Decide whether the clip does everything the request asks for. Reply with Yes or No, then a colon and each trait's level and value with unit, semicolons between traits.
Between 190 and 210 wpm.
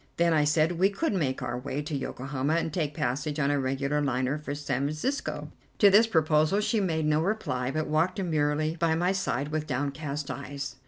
Yes: average, 200 wpm